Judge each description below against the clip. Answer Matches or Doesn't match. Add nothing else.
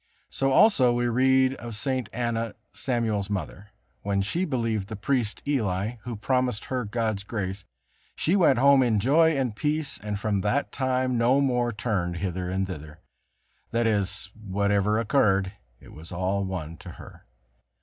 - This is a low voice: Matches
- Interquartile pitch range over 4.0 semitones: Matches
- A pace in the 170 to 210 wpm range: Doesn't match